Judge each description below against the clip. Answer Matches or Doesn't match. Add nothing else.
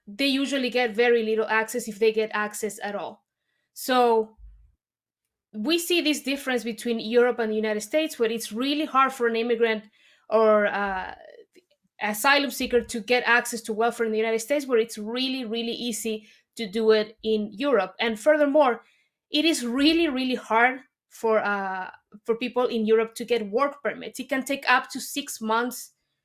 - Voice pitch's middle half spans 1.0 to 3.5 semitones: Matches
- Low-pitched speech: Doesn't match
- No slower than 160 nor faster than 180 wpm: Matches